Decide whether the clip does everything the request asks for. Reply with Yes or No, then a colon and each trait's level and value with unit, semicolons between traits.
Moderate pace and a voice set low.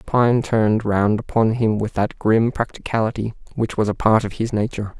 Yes: average, 190 wpm; low, 110 Hz